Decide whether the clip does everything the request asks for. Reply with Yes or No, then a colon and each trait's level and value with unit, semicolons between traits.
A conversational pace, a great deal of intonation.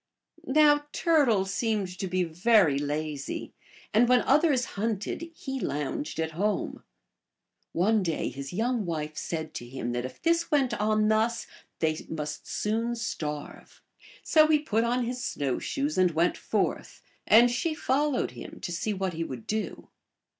Yes: average, 155 wpm; wide, 7.5 semitones